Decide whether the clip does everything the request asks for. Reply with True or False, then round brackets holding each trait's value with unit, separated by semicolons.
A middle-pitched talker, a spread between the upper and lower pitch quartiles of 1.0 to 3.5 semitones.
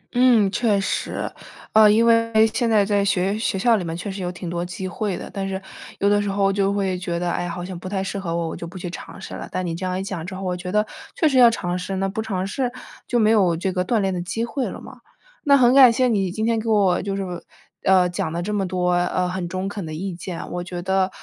False (195 Hz; 3.0 semitones)